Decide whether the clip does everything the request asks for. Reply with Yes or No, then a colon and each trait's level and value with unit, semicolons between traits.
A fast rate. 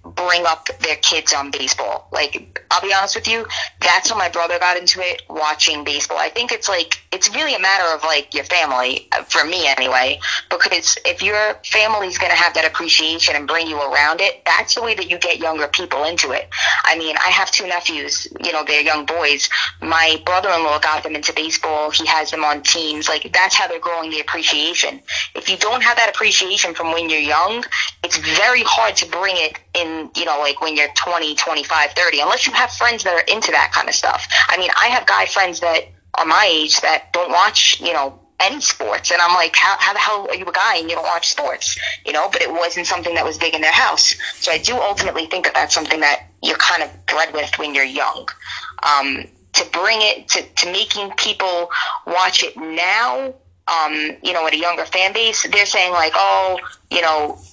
Yes: fast, 225 wpm